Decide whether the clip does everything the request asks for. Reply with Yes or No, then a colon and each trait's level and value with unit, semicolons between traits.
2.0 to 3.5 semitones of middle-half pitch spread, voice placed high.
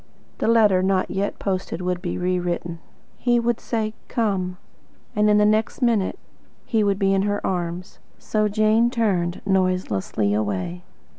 Yes: average, 3.2 semitones; high, 195 Hz